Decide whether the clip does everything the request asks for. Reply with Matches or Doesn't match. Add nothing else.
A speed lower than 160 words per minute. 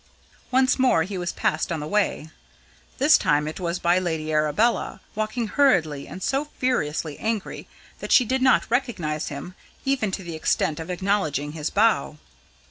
Doesn't match